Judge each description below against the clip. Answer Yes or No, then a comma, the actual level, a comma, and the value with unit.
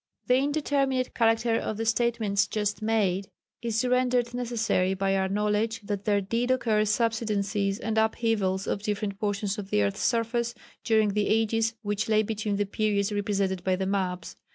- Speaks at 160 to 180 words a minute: Yes, average, 165 wpm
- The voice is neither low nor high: No, high, 215 Hz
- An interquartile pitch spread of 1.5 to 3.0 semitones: Yes, narrow, 2.4 semitones